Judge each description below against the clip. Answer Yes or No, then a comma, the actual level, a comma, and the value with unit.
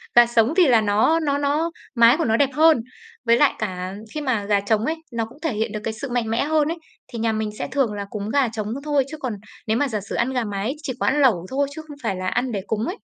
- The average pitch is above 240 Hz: No, high, 235 Hz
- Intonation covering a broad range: No, average, 4.8 semitones